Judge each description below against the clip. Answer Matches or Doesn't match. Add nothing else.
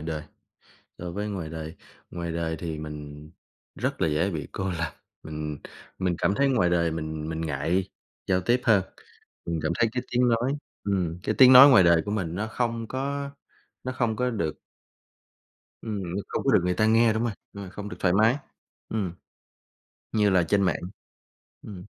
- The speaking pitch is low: Matches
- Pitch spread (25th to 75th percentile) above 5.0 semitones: Matches